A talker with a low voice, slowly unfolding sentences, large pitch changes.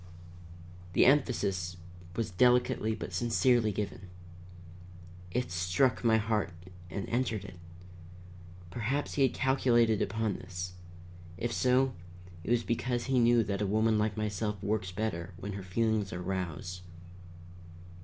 No: low, 110 Hz; slow, 130 wpm; average, 4.0 semitones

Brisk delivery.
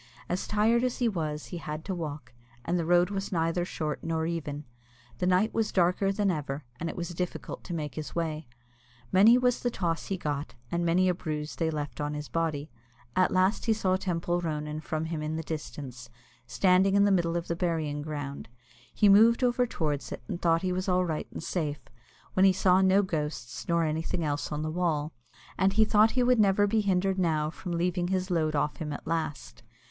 Yes: fast, 215 wpm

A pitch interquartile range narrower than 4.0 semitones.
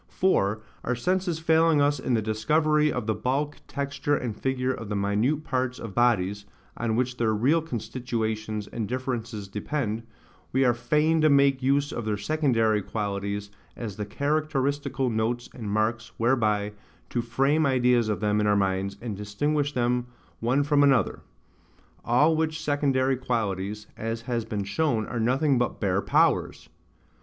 No: average, 4.8 semitones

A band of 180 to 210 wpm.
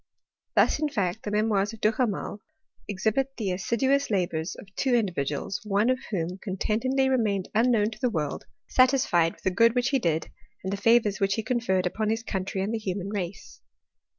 Yes: average, 190 wpm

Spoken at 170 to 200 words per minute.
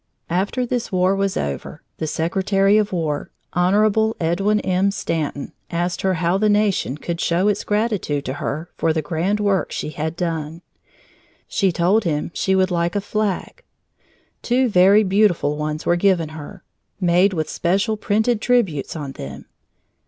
No: average, 160 wpm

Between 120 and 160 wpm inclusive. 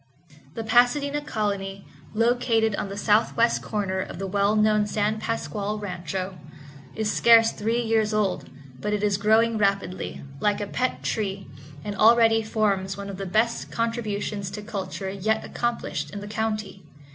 Yes: average, 155 wpm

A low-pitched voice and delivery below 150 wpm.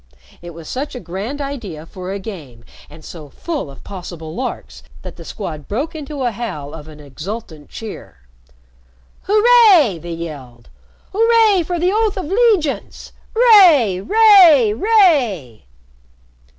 No: high, 225 Hz; slow, 135 wpm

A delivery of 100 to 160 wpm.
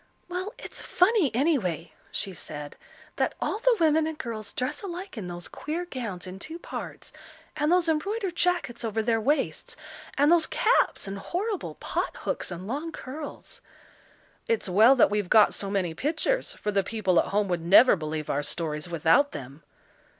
No: average, 170 wpm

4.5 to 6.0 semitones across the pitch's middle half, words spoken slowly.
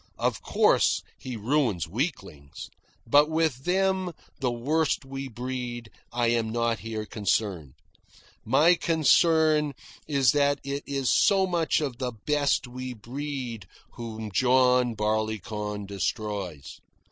Yes: average, 5.0 semitones; slow, 120 wpm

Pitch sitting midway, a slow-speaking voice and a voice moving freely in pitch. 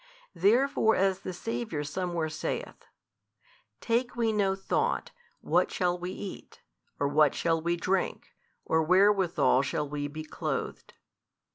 No: medium, 180 Hz; slow, 130 wpm; average, 4.1 semitones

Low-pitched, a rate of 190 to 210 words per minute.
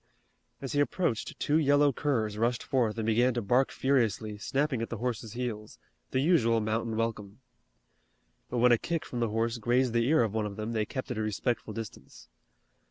Yes: low, 115 Hz; average, 195 wpm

